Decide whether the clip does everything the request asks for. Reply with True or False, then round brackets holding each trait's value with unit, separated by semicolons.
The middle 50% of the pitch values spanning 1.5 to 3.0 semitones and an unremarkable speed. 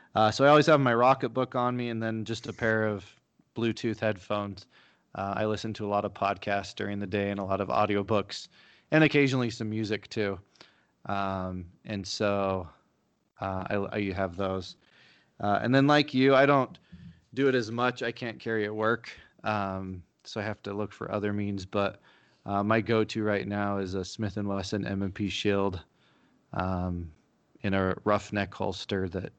True (2.4 semitones; 190 wpm)